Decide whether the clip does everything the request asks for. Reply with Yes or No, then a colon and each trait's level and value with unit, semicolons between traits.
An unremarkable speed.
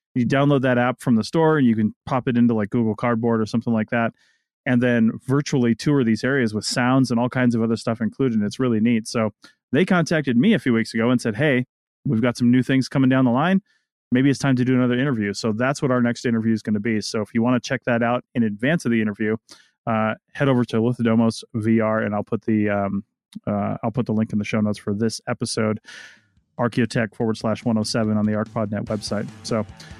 No: fast, 245 wpm